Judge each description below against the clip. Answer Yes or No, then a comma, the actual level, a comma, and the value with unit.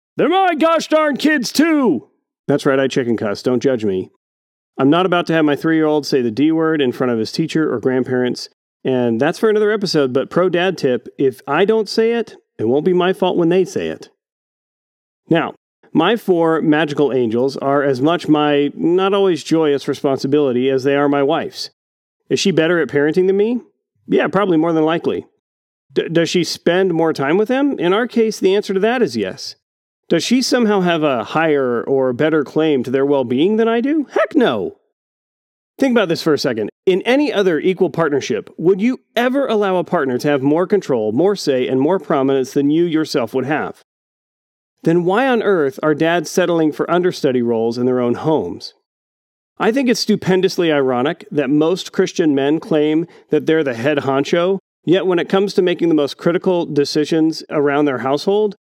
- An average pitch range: No, wide, 5.7 semitones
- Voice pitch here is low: No, medium, 160 Hz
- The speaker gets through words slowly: No, average, 200 wpm